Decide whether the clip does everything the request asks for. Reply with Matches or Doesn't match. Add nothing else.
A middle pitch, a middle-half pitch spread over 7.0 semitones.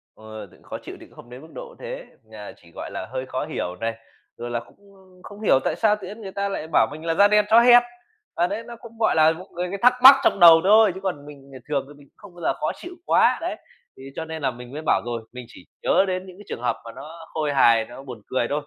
Matches